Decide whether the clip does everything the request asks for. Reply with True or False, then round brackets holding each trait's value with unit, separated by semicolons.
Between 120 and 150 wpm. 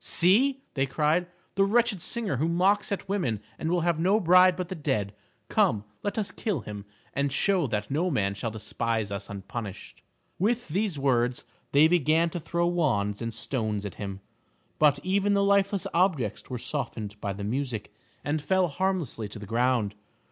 False (175 wpm)